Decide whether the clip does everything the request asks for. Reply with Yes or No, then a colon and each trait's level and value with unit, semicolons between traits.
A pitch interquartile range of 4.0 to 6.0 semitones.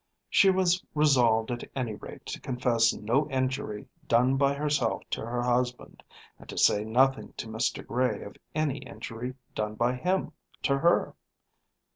No: average, 3.3 semitones